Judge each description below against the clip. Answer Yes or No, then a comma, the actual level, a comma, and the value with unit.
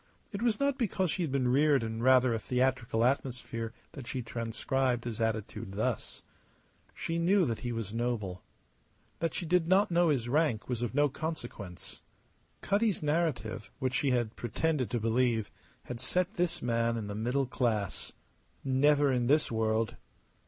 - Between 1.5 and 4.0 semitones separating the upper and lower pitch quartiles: No, average, 5.0 semitones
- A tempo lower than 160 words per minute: No, average, 165 wpm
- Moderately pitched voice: No, low, 125 Hz